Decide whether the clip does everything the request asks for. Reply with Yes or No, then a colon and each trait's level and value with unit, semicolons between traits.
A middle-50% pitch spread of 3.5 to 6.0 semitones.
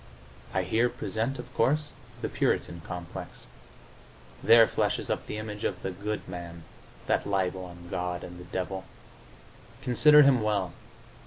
Yes: average, 4.7 semitones